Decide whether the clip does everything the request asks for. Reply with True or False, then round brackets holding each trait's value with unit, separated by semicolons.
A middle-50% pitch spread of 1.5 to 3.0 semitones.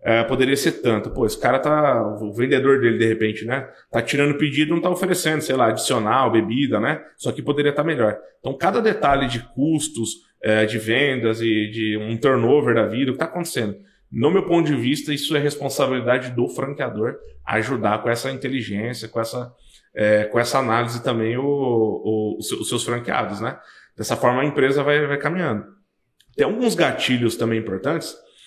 False (4.4 semitones)